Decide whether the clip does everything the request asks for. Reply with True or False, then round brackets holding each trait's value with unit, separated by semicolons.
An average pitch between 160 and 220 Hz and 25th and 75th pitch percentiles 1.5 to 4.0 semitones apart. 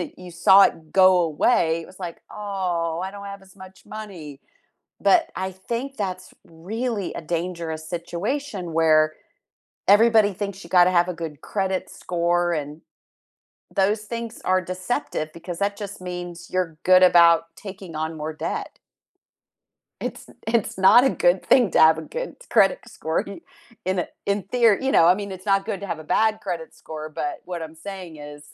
True (185 Hz; 3.3 semitones)